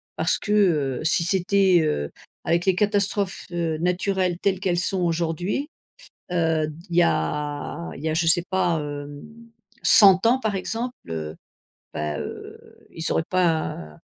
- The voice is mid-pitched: Yes, medium, 170 Hz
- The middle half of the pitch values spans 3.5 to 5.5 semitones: Yes, average, 3.9 semitones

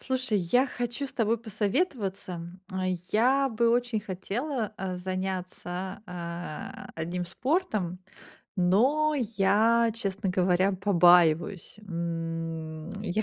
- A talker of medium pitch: No, high, 195 Hz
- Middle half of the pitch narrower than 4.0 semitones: No, average, 4.7 semitones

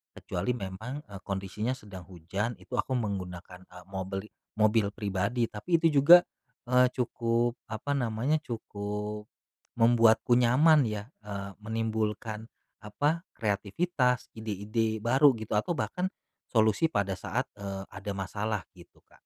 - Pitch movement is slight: No, average, 3.8 semitones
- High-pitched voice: No, low, 110 Hz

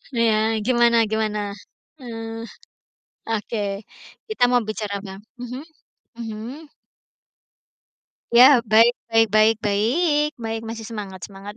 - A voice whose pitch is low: No, high, 225 Hz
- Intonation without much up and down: Yes, narrow, 2.0 semitones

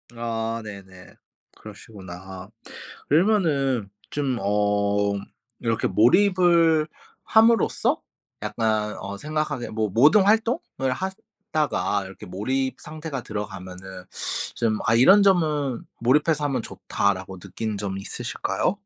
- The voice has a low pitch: Yes, low, 115 Hz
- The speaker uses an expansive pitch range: Yes, wide, 7.2 semitones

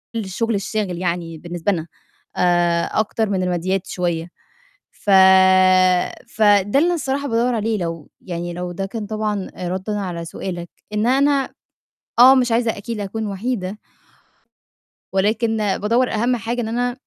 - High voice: Yes, high, 205 Hz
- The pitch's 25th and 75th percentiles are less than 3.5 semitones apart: No, average, 4.3 semitones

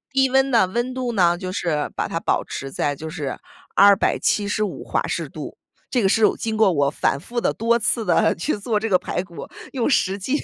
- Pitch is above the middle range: Yes, high, 205 Hz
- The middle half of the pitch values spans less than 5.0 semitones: No, average, 5.3 semitones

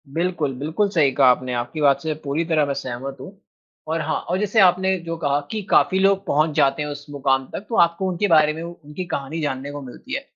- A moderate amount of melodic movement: Yes, average, 4.1 semitones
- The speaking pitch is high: No, medium, 155 Hz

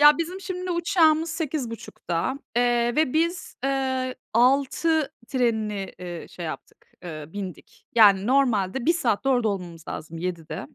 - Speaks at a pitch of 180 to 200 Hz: No, very high, 250 Hz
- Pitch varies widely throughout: Yes, wide, 8.1 semitones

